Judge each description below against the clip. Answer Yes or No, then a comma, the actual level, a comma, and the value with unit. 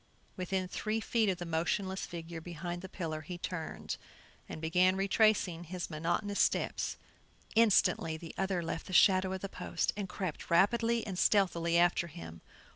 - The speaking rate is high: No, average, 160 wpm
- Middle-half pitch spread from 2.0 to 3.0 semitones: Yes, narrow, 2.5 semitones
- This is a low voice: No, medium, 180 Hz